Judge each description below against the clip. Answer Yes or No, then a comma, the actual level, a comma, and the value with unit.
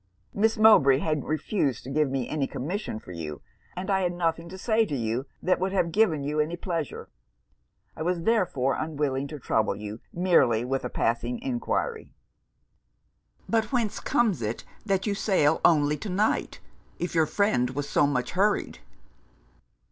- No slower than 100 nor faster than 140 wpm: No, average, 165 wpm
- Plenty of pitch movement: Yes, wide, 6.3 semitones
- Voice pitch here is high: No, medium, 160 Hz